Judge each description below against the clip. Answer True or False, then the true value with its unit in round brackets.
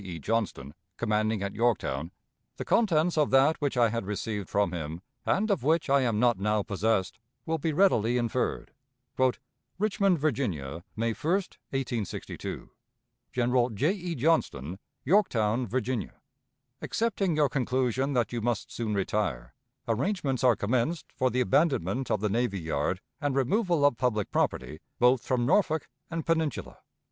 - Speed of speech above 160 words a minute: False (145 wpm)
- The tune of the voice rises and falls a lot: True (6.2 semitones)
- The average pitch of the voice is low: True (125 Hz)